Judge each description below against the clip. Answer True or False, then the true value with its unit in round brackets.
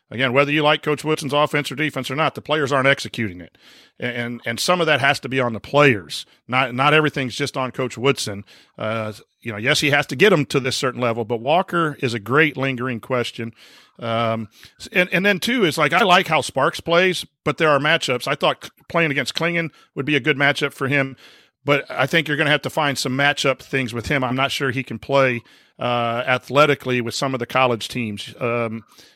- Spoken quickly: True (230 wpm)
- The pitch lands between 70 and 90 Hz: False (135 Hz)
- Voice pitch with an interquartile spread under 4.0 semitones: True (3.6 semitones)